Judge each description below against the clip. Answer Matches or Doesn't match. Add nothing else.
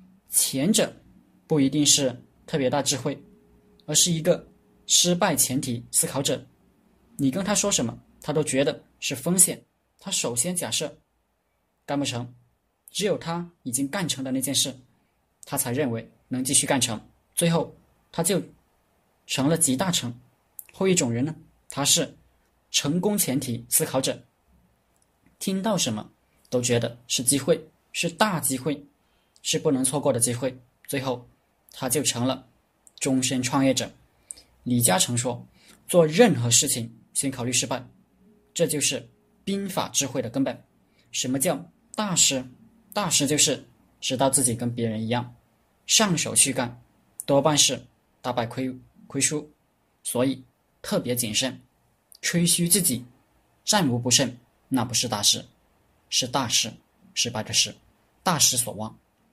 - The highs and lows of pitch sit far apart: Doesn't match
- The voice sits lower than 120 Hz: Doesn't match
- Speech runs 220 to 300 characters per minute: Doesn't match